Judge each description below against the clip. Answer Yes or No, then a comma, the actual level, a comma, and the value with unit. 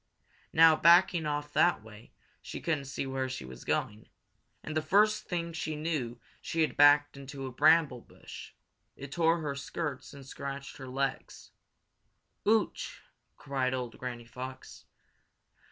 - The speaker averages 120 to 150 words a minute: Yes, average, 145 wpm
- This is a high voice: No, medium, 140 Hz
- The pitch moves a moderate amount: Yes, average, 3.7 semitones